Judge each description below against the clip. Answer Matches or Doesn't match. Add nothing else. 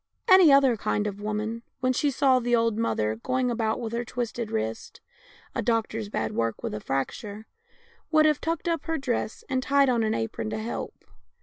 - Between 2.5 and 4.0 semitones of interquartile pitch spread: Doesn't match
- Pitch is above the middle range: Matches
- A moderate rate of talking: Doesn't match